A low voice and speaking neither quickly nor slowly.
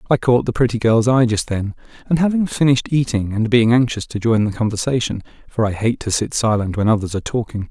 No: low, 115 Hz; fast, 225 wpm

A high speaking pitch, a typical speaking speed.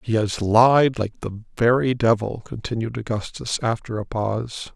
No: low, 115 Hz; average, 150 wpm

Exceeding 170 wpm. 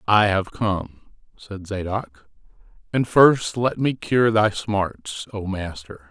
No: average, 140 wpm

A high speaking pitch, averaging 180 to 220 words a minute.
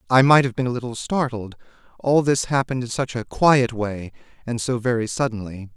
No: low, 120 Hz; average, 200 wpm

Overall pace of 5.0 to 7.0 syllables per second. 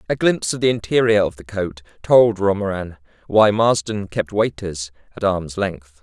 No: 4.7 syllables/s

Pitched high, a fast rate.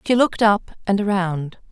No: high, 200 Hz; average, 175 wpm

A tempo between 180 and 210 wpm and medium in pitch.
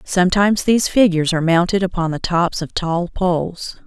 No: average, 170 wpm; medium, 180 Hz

